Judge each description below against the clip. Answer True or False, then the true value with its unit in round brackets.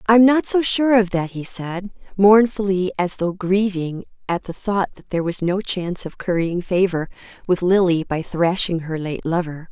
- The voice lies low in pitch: False (185 Hz)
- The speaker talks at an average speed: True (185 wpm)